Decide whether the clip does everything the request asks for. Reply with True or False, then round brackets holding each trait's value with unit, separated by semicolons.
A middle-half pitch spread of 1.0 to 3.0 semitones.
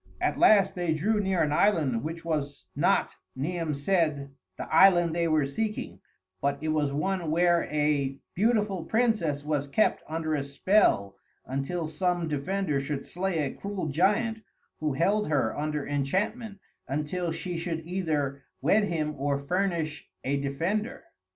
False (4.7 semitones)